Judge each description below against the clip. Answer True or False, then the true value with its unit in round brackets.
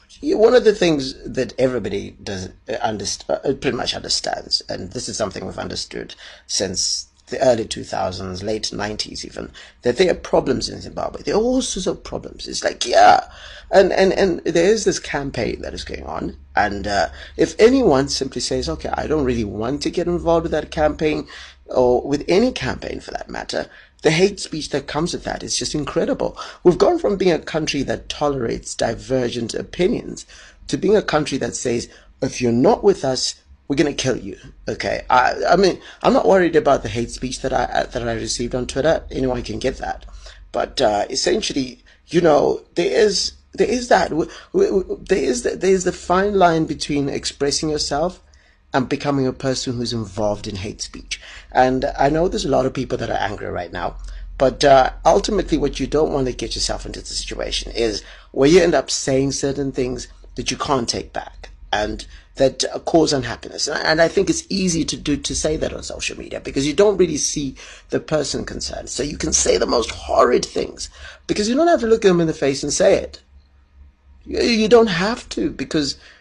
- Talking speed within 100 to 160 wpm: False (200 wpm)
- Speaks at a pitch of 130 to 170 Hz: True (140 Hz)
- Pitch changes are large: True (6.7 semitones)